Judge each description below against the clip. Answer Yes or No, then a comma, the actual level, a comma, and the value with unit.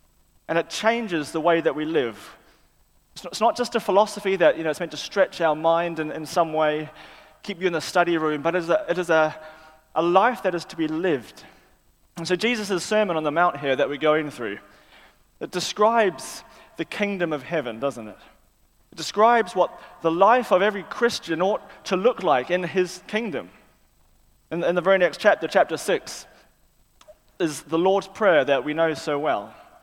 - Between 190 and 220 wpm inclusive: Yes, average, 200 wpm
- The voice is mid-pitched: Yes, medium, 170 Hz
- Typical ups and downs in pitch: Yes, average, 3.8 semitones